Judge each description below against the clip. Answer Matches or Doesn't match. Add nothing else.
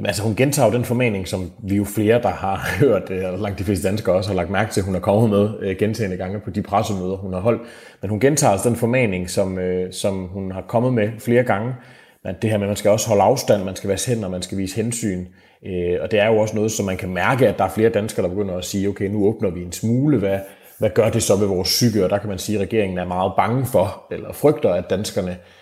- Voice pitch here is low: Matches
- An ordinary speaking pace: Doesn't match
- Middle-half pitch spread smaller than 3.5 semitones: Matches